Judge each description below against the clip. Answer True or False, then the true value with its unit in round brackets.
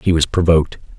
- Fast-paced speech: False (185 wpm)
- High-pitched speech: False (80 Hz)